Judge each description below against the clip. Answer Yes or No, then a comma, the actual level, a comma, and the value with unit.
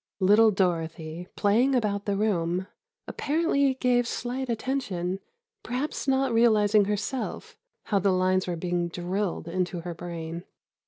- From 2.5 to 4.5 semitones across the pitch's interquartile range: No, wide, 5.4 semitones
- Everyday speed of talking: No, slow, 125 wpm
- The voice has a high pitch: Yes, high, 200 Hz